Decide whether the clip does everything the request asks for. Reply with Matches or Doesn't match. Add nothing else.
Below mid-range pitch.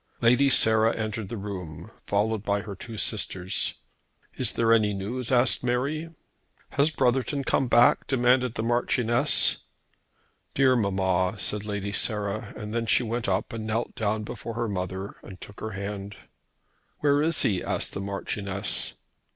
Matches